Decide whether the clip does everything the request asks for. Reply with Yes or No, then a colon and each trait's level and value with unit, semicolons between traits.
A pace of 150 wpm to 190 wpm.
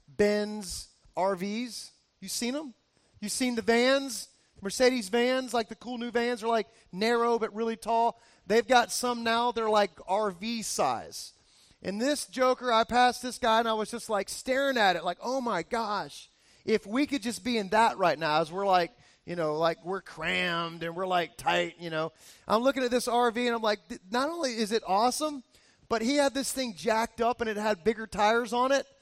No: fast, 205 wpm